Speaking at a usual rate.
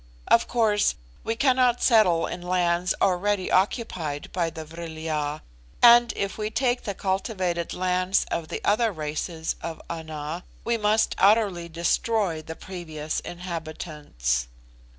No: slow, 130 wpm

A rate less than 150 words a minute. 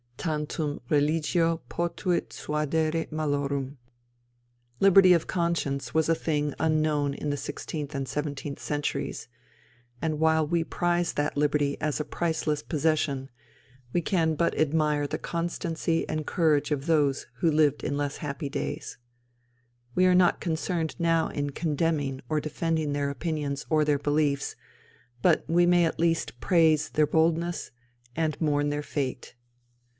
Yes: average, 140 wpm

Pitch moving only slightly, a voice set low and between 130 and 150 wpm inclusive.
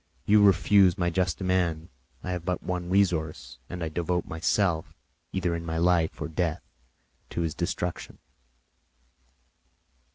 Yes: narrow, 1.8 semitones; very low, 90 Hz; slow, 135 wpm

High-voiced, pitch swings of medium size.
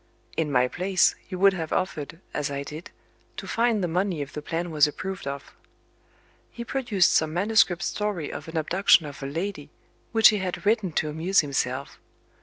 No: medium, 175 Hz; average, 4.7 semitones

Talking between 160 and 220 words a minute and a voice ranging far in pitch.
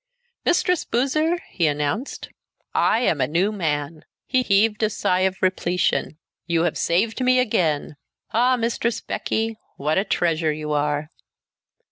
No: average, 140 wpm; wide, 6.9 semitones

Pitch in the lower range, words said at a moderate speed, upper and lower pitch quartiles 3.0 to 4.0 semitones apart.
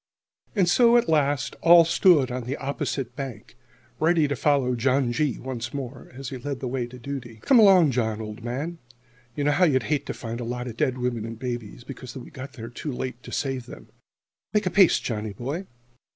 No: low, 130 Hz; fast, 210 wpm; average, 3.6 semitones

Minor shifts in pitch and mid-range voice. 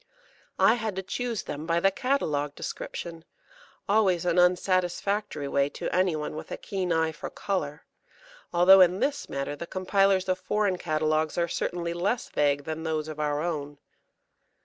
No: average, 3.7 semitones; medium, 175 Hz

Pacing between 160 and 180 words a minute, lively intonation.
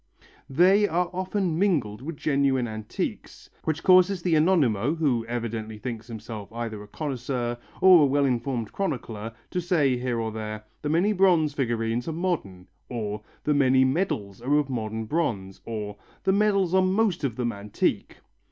Yes: average, 165 wpm; wide, 7.1 semitones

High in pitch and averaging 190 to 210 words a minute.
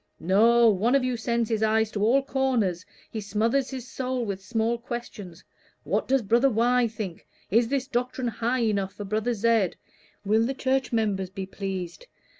No: high, 230 Hz; average, 175 wpm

